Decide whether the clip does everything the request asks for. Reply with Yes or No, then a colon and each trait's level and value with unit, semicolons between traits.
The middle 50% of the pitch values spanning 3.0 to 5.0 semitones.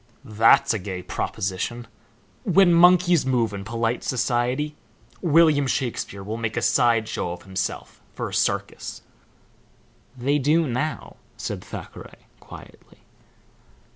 No: wide, 5.6 semitones